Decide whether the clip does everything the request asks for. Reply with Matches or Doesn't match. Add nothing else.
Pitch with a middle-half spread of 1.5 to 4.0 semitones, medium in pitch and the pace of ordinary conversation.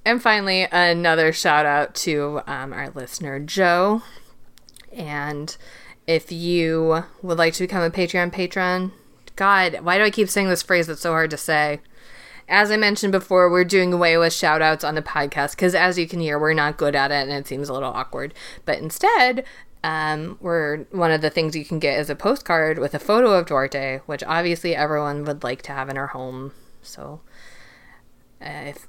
Matches